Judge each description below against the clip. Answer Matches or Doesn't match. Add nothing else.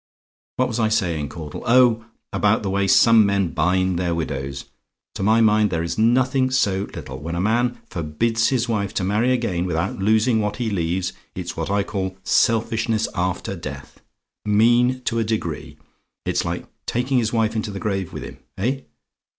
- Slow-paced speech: Doesn't match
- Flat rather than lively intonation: Doesn't match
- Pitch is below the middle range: Matches